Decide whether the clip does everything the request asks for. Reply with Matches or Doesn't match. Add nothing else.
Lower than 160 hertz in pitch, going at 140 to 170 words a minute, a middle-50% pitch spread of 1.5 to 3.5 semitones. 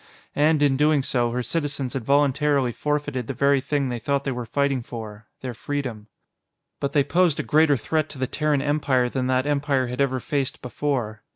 Doesn't match